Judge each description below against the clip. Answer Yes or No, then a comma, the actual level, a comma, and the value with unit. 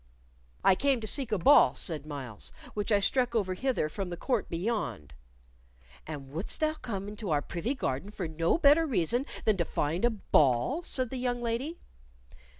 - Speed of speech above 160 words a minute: Yes, average, 180 wpm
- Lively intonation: Yes, wide, 7.4 semitones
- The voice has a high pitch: Yes, high, 205 Hz